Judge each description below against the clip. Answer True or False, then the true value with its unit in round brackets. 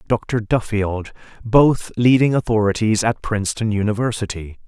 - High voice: False (110 Hz)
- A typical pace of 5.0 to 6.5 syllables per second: False (4.7 syllables/s)